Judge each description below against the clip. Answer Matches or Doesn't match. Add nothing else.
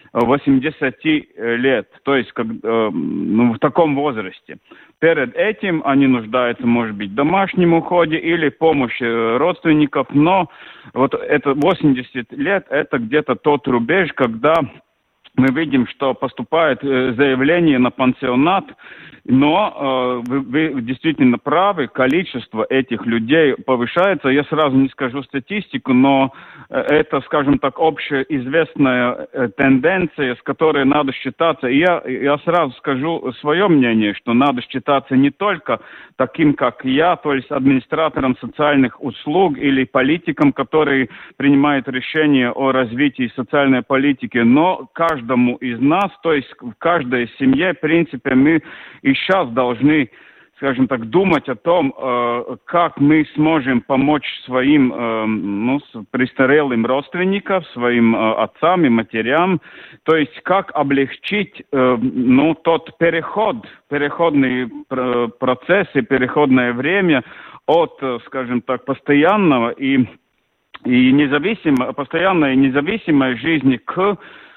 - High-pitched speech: Doesn't match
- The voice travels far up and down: Doesn't match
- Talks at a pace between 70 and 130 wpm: Matches